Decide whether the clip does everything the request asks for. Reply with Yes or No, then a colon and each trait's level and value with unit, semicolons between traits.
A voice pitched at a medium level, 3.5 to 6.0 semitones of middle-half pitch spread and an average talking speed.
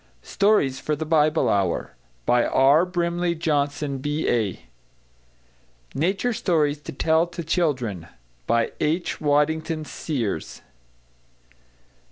No: medium, 150 Hz; average, 3.9 semitones; slow, 100 wpm